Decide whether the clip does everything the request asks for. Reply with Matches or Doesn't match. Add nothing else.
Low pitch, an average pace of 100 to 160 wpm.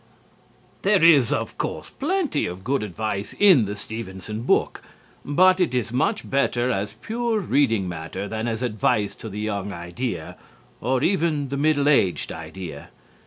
Matches